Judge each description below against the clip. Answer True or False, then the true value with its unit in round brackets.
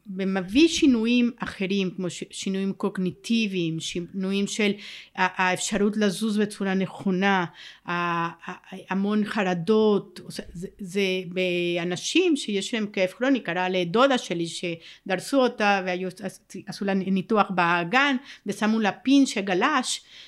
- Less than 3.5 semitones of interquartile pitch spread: True (2.7 semitones)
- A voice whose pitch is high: True (195 Hz)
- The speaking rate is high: False (100 wpm)